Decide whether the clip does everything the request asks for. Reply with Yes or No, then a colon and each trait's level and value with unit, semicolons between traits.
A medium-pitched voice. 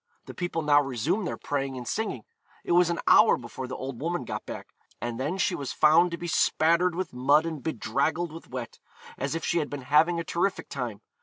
Yes: medium, 155 Hz